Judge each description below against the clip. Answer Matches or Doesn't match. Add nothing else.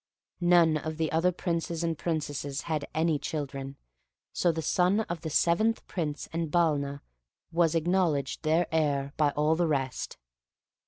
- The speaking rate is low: Doesn't match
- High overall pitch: Doesn't match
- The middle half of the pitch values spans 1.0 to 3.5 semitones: Matches